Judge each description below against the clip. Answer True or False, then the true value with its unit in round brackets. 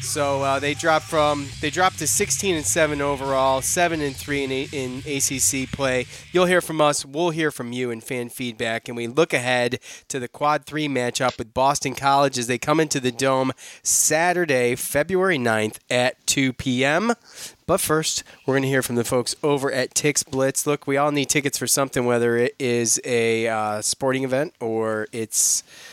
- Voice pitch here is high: False (135 Hz)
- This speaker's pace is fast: False (195 wpm)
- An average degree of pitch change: True (3.1 semitones)